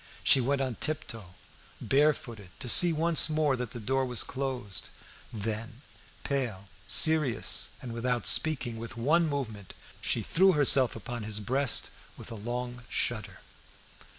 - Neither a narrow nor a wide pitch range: Yes, average, 3.8 semitones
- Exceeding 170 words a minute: No, average, 140 wpm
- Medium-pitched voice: No, low, 125 Hz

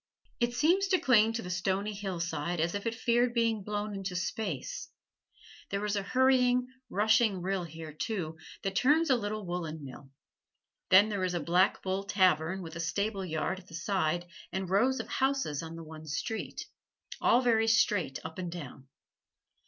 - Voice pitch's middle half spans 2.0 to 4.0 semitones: No, average, 4.9 semitones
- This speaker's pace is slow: No, average, 175 wpm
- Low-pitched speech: No, high, 195 Hz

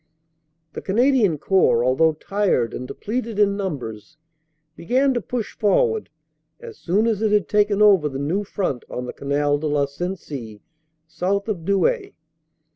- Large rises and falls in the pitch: Yes, wide, 6.6 semitones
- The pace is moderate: Yes, average, 150 wpm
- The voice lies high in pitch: Yes, high, 195 Hz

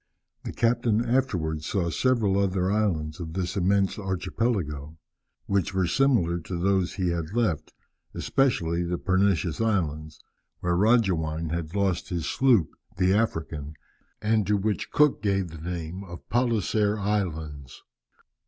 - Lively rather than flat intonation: No, average, 4.3 semitones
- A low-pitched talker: Yes, very low, 95 Hz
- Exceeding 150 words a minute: No, slow, 135 wpm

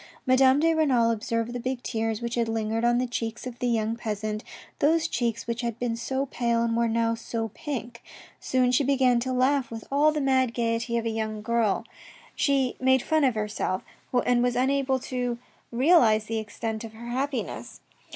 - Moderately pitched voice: No, high, 240 Hz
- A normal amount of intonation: No, narrow, 2.3 semitones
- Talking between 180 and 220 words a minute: Yes, average, 190 wpm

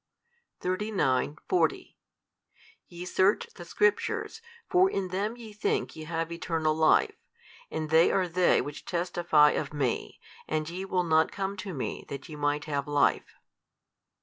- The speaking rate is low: No, average, 150 wpm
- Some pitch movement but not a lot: Yes, average, 3.8 semitones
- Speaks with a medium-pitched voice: Yes, medium, 170 Hz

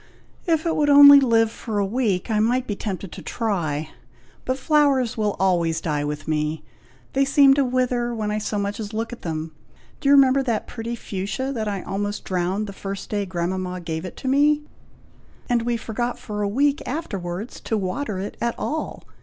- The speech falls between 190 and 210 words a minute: Yes, average, 195 wpm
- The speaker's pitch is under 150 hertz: No, high, 220 Hz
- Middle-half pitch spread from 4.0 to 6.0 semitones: Yes, wide, 5.4 semitones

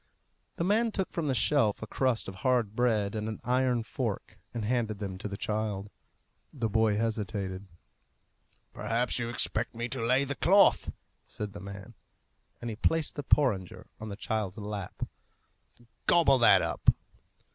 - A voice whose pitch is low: Yes, low, 110 Hz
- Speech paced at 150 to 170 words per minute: Yes, average, 160 wpm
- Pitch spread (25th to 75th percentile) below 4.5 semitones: Yes, average, 3.6 semitones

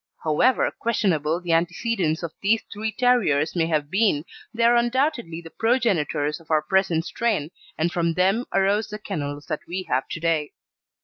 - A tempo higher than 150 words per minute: Yes, average, 170 wpm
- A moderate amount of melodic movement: No, wide, 5.9 semitones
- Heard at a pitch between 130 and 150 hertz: No, medium, 175 Hz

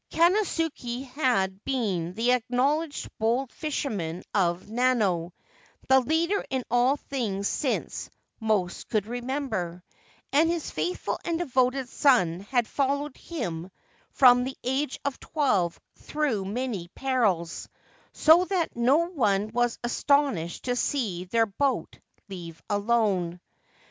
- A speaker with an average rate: No, slow, 120 wpm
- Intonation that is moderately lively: No, wide, 6.0 semitones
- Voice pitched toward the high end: Yes, high, 245 Hz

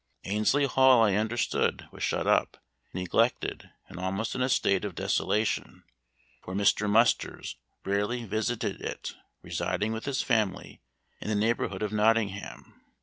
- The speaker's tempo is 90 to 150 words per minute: Yes, average, 140 wpm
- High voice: No, low, 110 Hz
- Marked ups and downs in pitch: No, narrow, 2.6 semitones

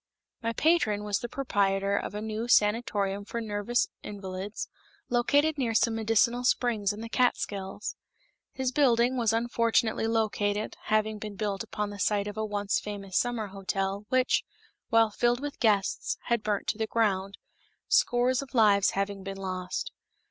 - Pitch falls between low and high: No, high, 215 Hz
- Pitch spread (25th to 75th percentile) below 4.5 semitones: Yes, average, 2.8 semitones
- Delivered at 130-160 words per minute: Yes, average, 155 wpm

